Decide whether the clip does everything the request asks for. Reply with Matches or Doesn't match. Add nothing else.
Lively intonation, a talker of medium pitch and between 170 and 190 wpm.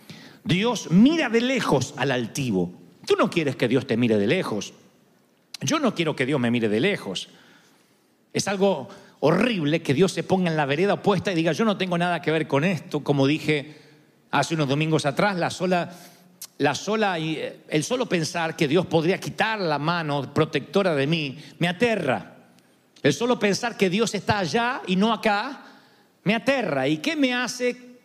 Matches